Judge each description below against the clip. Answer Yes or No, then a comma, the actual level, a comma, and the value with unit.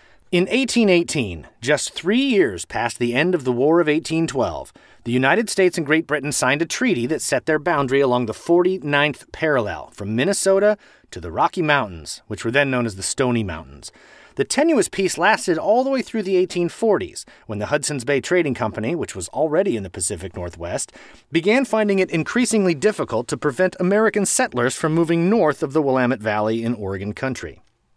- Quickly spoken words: No, average, 185 wpm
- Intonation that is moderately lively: No, wide, 7.6 semitones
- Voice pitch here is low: No, medium, 150 Hz